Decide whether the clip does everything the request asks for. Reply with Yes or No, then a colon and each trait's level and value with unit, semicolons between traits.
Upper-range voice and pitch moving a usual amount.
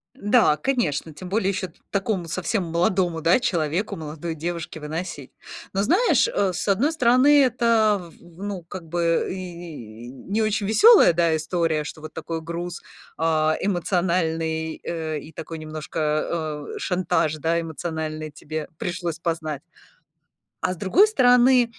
No: medium, 170 Hz; average, 3.9 semitones